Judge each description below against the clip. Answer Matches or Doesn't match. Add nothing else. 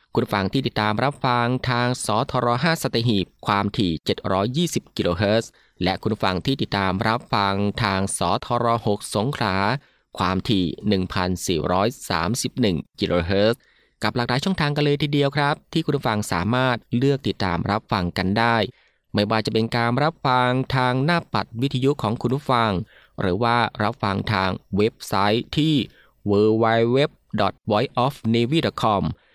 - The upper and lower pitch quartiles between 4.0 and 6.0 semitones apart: Matches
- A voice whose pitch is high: Doesn't match